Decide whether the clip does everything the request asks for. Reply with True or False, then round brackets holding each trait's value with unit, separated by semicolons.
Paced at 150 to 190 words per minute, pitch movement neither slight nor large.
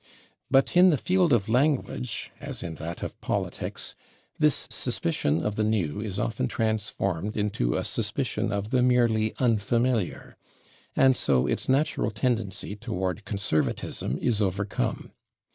False (135 wpm; 4.3 semitones)